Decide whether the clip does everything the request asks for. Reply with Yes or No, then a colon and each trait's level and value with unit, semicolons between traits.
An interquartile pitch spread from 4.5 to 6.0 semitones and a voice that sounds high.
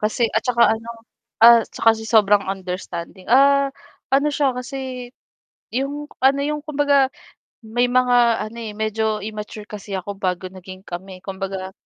Yes: average, 5.0 semitones; high, 220 Hz